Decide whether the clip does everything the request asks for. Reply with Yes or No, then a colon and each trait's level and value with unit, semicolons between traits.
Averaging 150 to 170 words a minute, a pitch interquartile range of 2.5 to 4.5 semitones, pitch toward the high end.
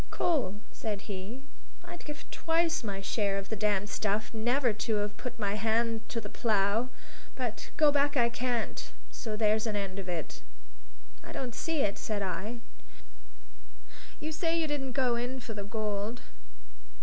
Yes: average, 165 wpm; average, 4.0 semitones; high, 225 Hz